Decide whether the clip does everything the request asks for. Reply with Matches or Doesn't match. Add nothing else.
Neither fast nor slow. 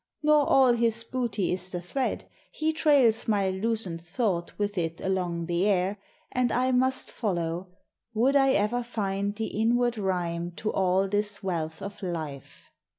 Matches